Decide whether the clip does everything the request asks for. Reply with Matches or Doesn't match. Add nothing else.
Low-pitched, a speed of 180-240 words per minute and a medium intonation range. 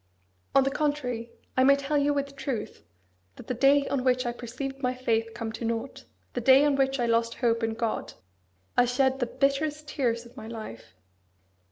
Doesn't match